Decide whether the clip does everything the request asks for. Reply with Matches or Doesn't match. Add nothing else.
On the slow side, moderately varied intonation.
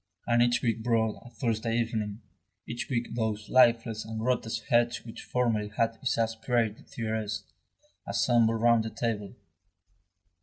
Doesn't match